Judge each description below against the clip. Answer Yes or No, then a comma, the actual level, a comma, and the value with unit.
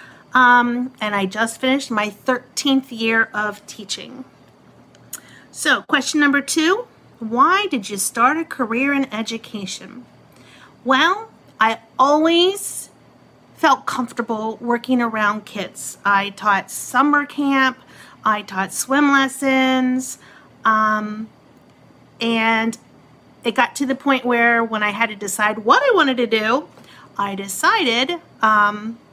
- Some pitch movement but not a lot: Yes, average, 3.8 semitones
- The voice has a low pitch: No, high, 240 Hz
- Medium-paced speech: No, slow, 120 wpm